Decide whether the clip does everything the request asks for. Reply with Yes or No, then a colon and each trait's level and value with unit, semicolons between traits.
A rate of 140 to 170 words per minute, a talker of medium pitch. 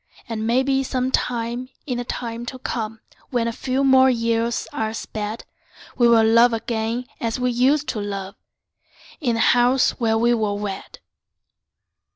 No: average, 155 wpm; high, 235 Hz